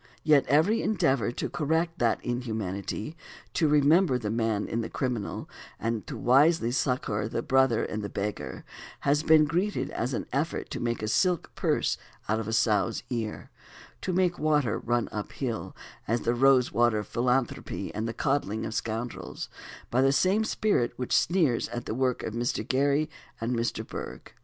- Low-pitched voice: Yes, low, 125 Hz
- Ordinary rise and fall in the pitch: Yes, average, 4.7 semitones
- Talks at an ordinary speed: Yes, average, 165 wpm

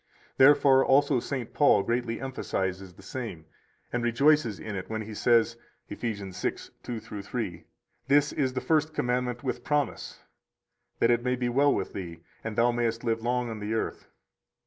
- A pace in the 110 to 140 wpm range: No, average, 170 wpm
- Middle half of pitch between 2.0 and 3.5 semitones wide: Yes, average, 3.2 semitones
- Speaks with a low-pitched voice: Yes, low, 120 Hz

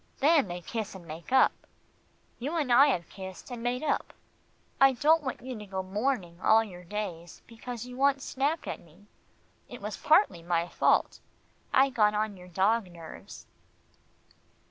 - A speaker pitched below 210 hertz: No, high, 220 Hz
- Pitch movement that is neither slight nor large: No, wide, 6.6 semitones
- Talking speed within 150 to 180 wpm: Yes, average, 165 wpm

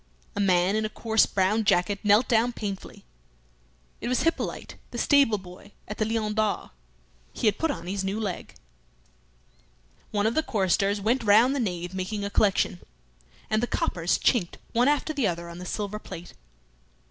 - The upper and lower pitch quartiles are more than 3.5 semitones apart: No, average, 3.1 semitones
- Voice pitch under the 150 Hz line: No, high, 210 Hz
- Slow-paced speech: No, average, 175 wpm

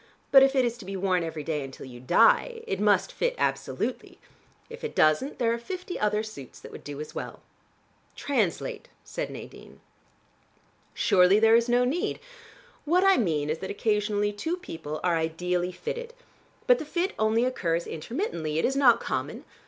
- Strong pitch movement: Yes, wide, 8.6 semitones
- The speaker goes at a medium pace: Yes, average, 175 wpm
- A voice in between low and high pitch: No, high, 210 Hz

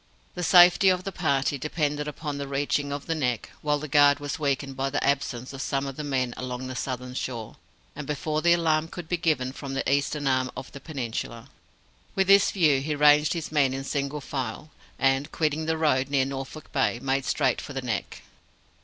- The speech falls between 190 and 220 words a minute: Yes, fast, 205 wpm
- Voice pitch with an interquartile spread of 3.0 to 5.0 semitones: No, narrow, 2.5 semitones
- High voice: No, medium, 140 Hz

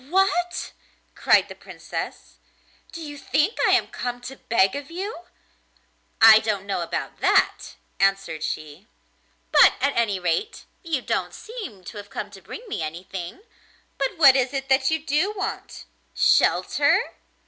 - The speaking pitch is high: Yes, very high, 260 Hz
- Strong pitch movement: Yes, wide, 8.8 semitones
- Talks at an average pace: Yes, average, 150 wpm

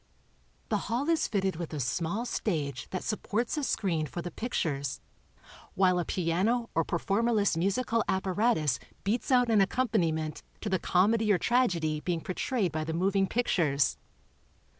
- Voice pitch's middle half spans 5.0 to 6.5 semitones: Yes, wide, 5.6 semitones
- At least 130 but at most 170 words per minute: Yes, average, 150 wpm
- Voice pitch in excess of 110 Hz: Yes, high, 190 Hz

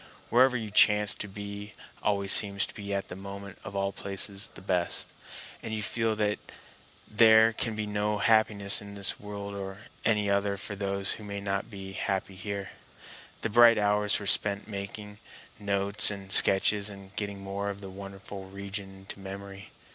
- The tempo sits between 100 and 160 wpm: No, average, 175 wpm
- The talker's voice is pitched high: No, low, 100 Hz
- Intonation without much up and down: Yes, narrow, 1.1 semitones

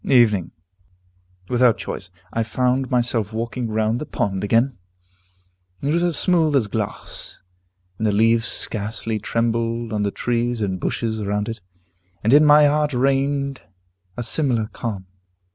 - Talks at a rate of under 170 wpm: Yes, average, 145 wpm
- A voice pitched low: Yes, low, 115 Hz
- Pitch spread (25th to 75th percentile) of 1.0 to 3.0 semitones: No, average, 3.6 semitones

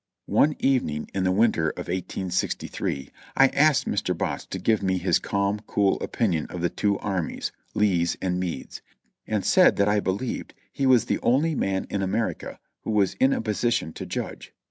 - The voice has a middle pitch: No, low, 100 Hz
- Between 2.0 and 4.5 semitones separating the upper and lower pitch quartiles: Yes, average, 4.0 semitones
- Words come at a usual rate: Yes, average, 180 wpm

